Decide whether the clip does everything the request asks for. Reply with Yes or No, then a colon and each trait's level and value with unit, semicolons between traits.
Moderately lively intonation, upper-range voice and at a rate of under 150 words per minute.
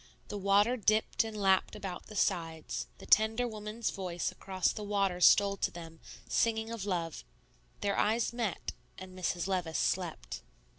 No: average, 3.1 semitones; high, 200 Hz; average, 155 wpm